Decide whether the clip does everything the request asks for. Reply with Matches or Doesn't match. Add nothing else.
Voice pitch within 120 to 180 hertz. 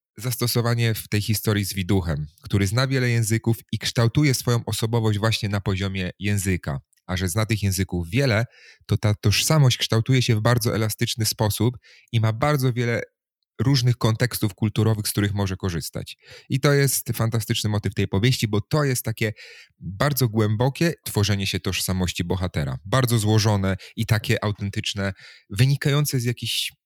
Doesn't match